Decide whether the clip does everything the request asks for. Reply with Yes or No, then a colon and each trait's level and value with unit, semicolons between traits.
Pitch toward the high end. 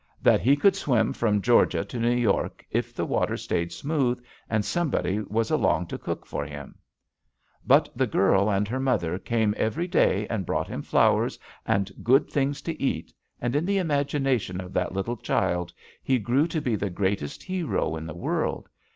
No: low, 115 Hz